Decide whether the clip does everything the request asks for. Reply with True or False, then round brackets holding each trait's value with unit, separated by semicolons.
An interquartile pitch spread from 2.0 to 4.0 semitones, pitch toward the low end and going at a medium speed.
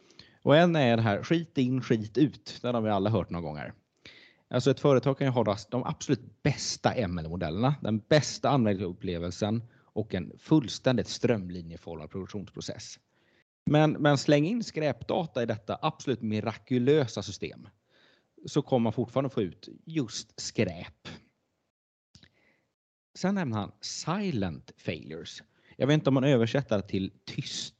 False (5.4 semitones; 120 Hz; 140 wpm)